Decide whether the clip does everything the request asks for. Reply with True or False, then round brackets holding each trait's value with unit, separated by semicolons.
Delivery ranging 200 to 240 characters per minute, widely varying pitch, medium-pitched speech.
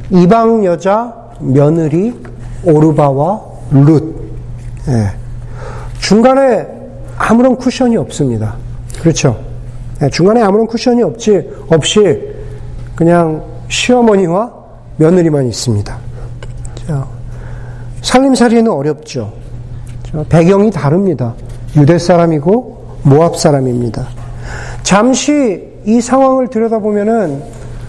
True (210 characters per minute; 9.0 semitones; 145 Hz)